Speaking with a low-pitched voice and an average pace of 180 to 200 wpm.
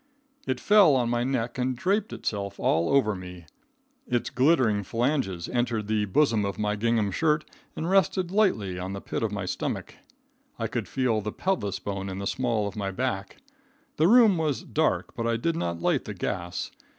Yes: low, 115 Hz; average, 185 wpm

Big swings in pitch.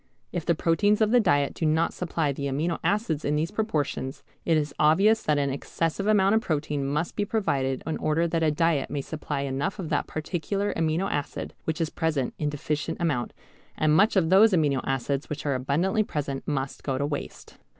No: average, 3.7 semitones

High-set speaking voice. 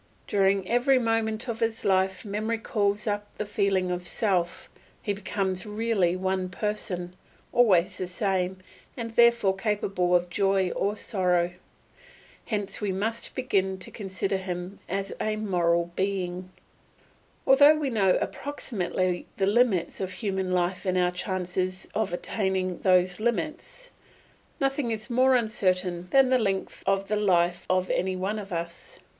Yes: high, 195 Hz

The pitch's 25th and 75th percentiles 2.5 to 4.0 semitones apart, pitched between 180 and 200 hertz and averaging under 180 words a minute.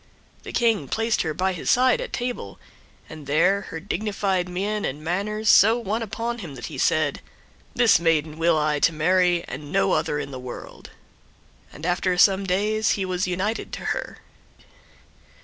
No: average, 4.9 semitones; medium, 185 Hz; average, 170 wpm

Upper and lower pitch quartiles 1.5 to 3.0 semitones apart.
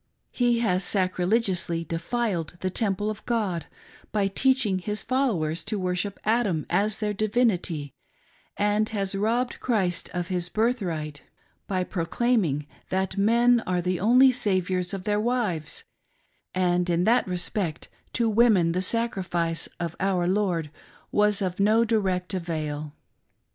No: average, 3.7 semitones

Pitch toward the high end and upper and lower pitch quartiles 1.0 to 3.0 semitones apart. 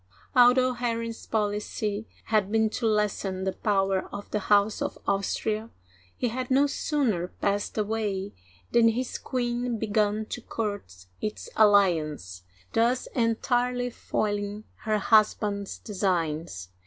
Yes: high, 215 Hz; narrow, 2.4 semitones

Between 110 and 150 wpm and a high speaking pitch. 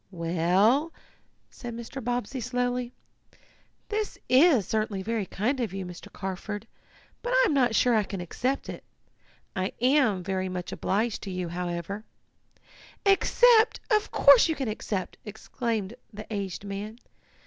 Yes: average, 145 wpm; high, 220 Hz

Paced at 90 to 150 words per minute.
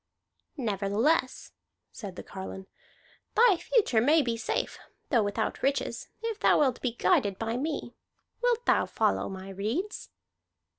Yes: slow, 135 wpm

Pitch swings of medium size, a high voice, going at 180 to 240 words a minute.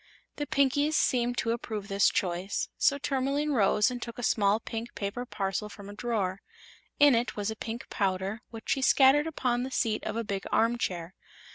Yes: average, 4.2 semitones; high, 230 Hz; average, 185 wpm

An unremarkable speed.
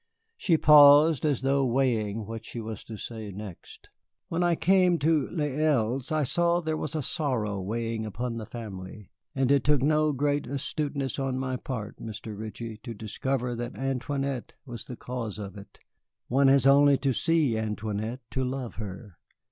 Yes: average, 175 wpm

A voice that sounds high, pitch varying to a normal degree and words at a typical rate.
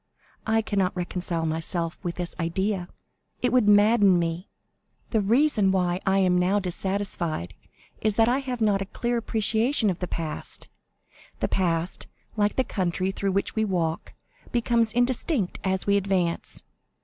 Yes: high, 195 Hz; average, 3.7 semitones; average, 150 wpm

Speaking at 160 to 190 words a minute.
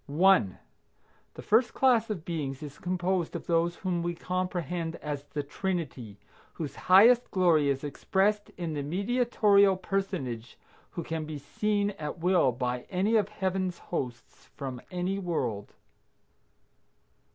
No: slow, 135 wpm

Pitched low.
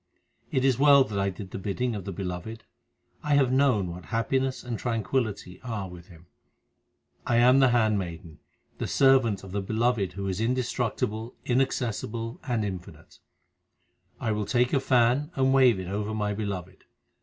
Yes: low, 110 Hz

